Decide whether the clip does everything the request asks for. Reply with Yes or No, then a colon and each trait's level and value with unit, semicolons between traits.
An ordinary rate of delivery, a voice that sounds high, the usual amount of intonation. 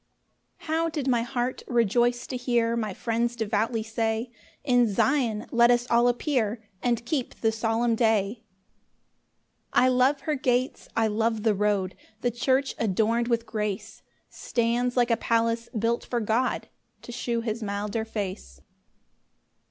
No: average, 150 wpm; high, 235 Hz; narrow, 1.9 semitones